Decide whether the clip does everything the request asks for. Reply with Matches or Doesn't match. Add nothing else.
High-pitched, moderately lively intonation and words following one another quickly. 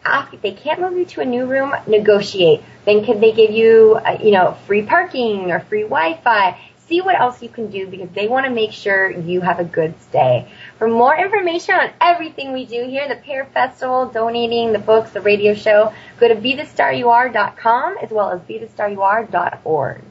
Doesn't match